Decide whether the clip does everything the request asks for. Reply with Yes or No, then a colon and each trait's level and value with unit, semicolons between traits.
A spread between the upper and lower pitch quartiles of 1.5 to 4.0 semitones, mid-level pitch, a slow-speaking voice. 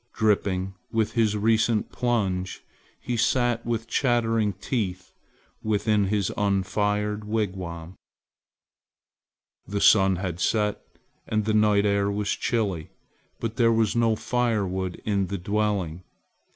No: average, 2.7 semitones; low, 105 Hz; slow, 120 wpm